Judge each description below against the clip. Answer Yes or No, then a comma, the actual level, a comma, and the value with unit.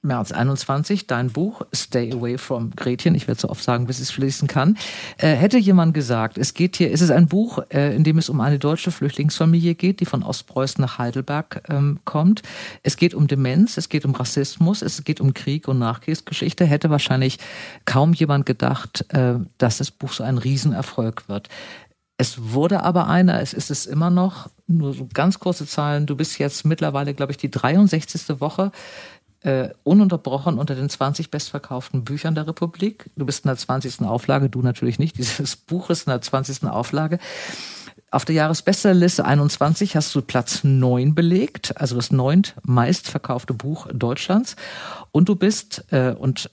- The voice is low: No, medium, 145 Hz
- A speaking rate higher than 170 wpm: Yes, average, 180 wpm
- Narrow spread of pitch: No, average, 4.5 semitones